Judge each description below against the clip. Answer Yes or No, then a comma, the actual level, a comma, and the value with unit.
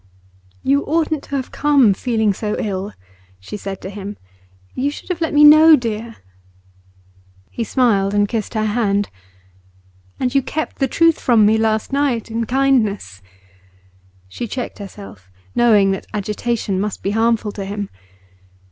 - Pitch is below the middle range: No, high, 220 Hz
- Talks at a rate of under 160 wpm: Yes, average, 150 wpm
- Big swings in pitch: No, average, 4.7 semitones